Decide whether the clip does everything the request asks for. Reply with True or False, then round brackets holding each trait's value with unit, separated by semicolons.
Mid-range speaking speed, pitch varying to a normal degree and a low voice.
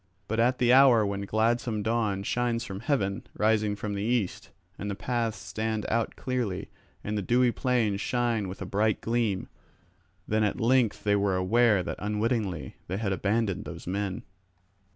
True (170 wpm; 3.0 semitones; 110 Hz)